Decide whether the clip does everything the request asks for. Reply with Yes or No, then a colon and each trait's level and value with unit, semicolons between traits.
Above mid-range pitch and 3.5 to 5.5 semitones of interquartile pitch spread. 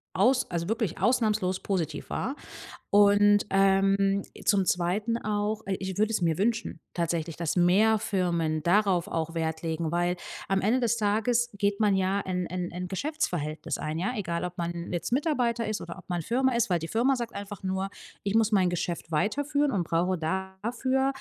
Yes: high, 195 Hz; average, 4.2 semitones